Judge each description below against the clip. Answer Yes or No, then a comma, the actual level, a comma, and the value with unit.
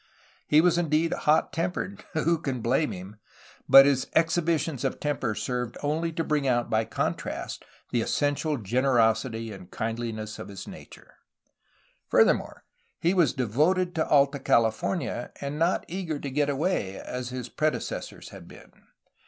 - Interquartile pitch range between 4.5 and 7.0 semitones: Yes, average, 5.3 semitones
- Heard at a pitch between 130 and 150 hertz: Yes, medium, 140 Hz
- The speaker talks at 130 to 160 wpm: Yes, average, 150 wpm